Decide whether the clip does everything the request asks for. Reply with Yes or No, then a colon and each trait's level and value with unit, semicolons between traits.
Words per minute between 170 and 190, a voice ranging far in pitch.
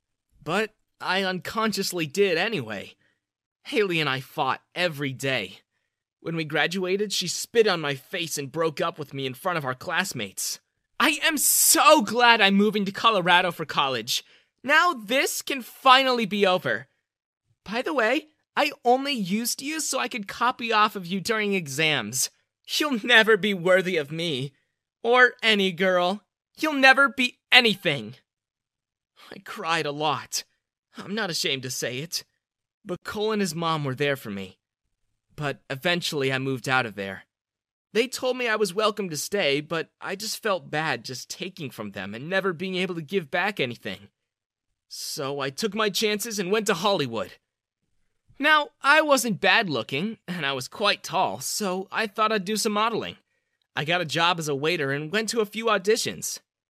Yes: average, 175 wpm; wide, 7.3 semitones